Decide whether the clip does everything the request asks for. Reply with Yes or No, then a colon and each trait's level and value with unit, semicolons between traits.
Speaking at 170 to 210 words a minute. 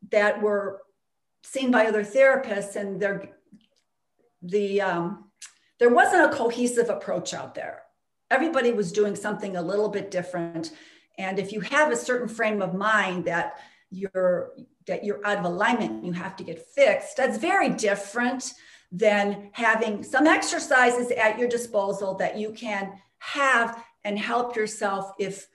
No: average, 150 wpm